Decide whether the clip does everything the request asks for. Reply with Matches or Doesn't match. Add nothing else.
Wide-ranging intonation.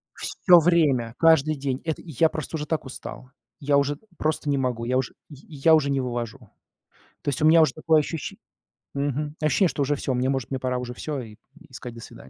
Doesn't match